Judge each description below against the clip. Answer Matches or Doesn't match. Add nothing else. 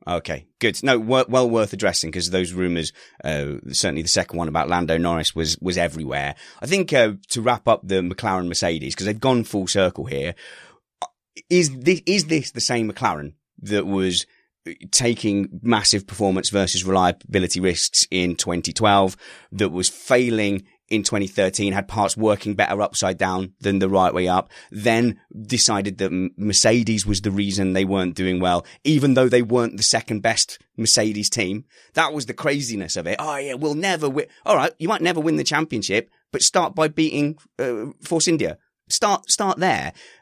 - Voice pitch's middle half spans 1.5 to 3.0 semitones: Doesn't match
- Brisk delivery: Doesn't match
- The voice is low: Matches